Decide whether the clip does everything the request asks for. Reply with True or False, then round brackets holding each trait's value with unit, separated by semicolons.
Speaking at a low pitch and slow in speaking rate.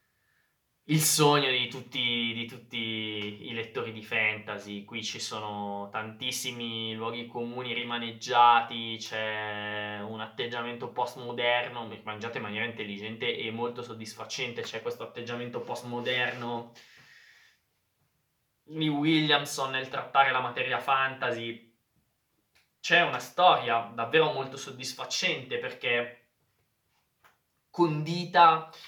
True (120 Hz; 100 wpm)